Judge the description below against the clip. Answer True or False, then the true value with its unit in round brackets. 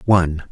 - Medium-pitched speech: False (90 Hz)